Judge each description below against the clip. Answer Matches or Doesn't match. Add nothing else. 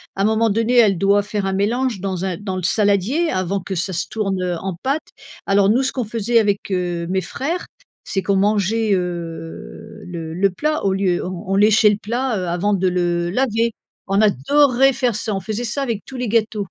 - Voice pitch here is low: Doesn't match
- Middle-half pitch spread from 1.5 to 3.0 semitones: Doesn't match